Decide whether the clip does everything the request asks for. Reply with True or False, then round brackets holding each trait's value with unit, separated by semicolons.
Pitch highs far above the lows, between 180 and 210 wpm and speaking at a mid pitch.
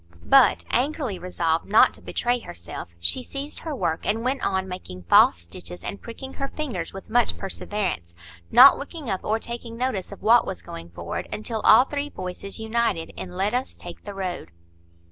False (5.9 semitones; 185 wpm; 205 Hz)